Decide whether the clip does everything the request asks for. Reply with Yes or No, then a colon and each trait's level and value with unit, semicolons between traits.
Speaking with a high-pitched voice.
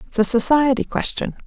Yes: very high, 255 Hz